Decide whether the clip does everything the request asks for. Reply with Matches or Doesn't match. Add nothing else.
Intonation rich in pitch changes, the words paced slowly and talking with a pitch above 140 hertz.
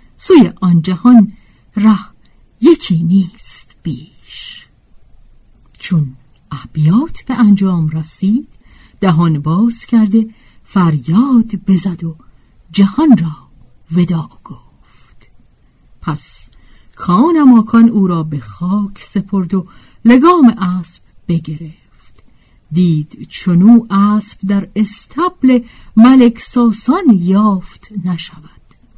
Matches